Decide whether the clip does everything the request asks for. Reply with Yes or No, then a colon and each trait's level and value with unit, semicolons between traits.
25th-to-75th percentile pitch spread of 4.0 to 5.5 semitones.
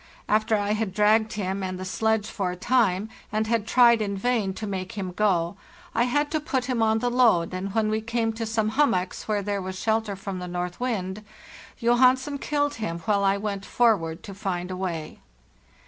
No: average, 3.4 semitones